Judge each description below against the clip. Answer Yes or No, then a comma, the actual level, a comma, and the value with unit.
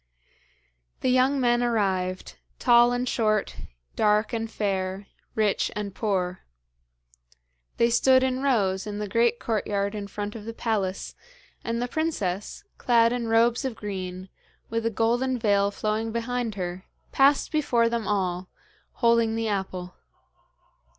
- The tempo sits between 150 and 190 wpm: No, slow, 135 wpm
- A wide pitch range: No, average, 3.1 semitones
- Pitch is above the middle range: Yes, high, 220 Hz